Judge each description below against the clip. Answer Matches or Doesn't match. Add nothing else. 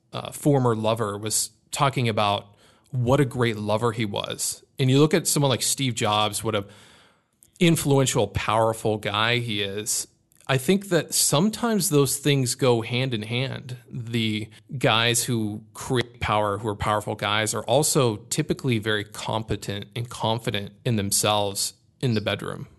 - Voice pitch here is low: Matches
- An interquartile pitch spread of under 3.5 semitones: Doesn't match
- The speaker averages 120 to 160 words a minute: Matches